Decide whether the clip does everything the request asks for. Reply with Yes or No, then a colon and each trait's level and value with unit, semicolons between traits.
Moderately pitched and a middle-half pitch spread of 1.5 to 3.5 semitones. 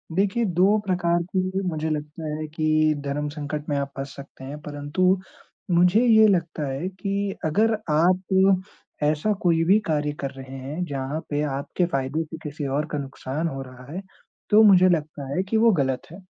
No: medium, 155 Hz; average, 4.4 semitones